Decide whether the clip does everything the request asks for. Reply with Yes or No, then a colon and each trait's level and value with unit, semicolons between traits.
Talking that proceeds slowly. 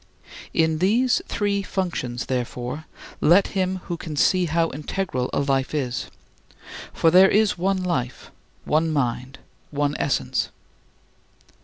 Yes: slow, 125 wpm